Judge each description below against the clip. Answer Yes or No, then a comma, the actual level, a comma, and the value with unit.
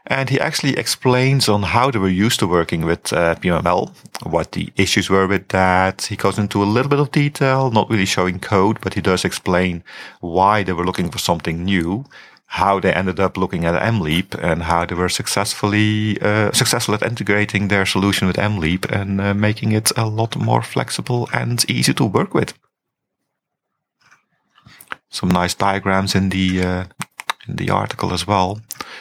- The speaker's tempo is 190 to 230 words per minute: No, average, 180 wpm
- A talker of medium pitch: No, low, 100 Hz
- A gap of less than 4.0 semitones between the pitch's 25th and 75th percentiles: Yes, average, 2.7 semitones